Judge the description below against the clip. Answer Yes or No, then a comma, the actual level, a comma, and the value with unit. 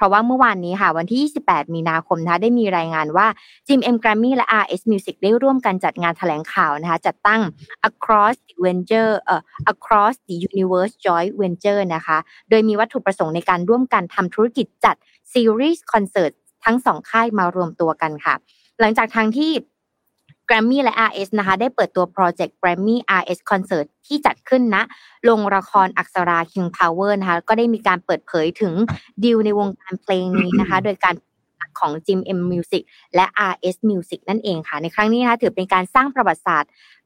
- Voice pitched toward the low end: No, high, 195 Hz